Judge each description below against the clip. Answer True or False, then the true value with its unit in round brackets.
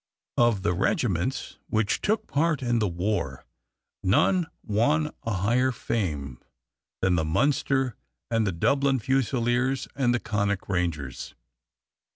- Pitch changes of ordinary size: False (5.9 semitones)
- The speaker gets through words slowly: True (125 wpm)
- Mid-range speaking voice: False (115 Hz)